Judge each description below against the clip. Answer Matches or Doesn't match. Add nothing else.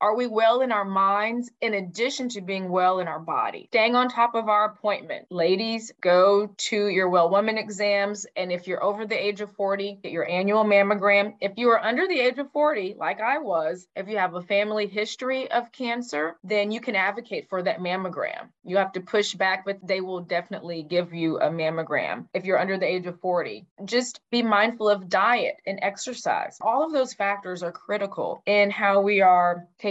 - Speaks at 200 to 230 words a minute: Matches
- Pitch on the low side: Doesn't match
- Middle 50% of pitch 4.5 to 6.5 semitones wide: Doesn't match